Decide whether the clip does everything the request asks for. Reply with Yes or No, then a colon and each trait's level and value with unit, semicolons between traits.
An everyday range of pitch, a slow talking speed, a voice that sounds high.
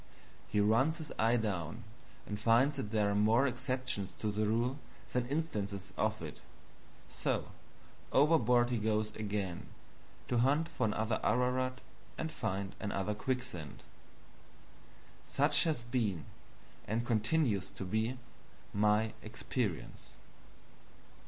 No: average, 3.6 semitones; slow, 120 wpm; low, 110 Hz